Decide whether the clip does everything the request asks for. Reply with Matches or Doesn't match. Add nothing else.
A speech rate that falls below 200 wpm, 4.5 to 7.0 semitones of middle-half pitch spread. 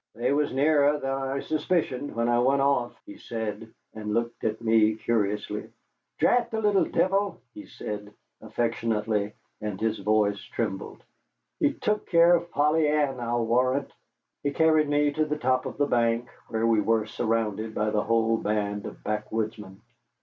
Matches